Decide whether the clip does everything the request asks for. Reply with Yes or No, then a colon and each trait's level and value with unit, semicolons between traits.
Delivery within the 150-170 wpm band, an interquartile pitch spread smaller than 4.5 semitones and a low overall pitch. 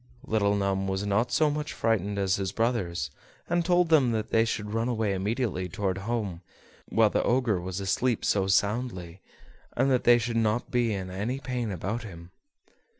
No: average, 180 wpm; average, 3.8 semitones; low, 105 Hz